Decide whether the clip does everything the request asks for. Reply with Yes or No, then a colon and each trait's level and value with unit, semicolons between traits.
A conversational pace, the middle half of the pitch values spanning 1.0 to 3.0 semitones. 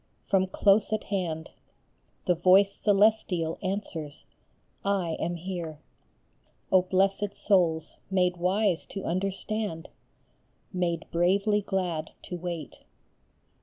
No: slow, 110 wpm; narrow, 2.6 semitones